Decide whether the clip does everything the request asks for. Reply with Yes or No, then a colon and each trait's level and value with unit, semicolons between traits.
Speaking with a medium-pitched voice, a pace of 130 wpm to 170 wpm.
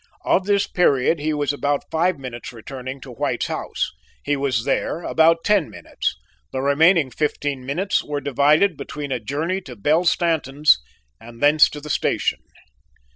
Yes: medium, 145 Hz; average, 160 wpm